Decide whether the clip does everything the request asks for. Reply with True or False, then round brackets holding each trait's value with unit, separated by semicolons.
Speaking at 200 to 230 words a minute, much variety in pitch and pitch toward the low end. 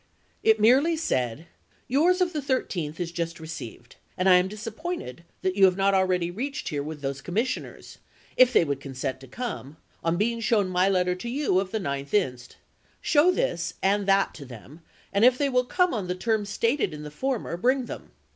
False (205 wpm; 7.5 semitones; 195 Hz)